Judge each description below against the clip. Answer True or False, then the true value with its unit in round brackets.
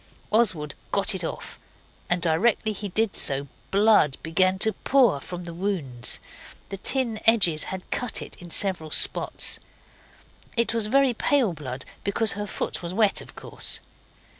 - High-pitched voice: True (195 Hz)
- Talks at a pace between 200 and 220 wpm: False (155 wpm)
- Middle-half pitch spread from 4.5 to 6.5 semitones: True (4.9 semitones)